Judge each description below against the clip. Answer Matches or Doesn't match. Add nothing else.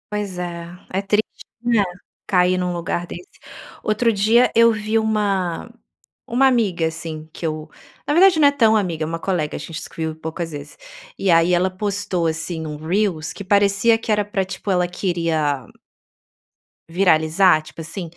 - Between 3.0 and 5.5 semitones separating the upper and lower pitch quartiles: Matches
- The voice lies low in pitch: Doesn't match